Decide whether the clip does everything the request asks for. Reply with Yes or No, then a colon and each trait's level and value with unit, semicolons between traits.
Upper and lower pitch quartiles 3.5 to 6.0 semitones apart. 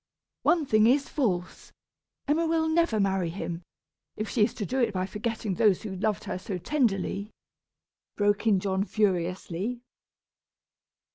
Yes: average, 4.2 semitones